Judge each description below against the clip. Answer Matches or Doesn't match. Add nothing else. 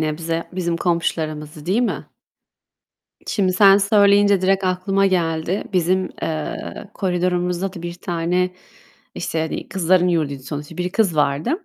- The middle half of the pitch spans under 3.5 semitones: Matches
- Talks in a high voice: Doesn't match